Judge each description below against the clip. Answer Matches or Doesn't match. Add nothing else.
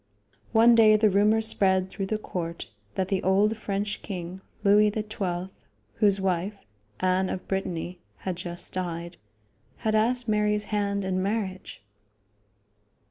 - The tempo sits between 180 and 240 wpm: Doesn't match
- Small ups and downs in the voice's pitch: Matches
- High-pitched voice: Matches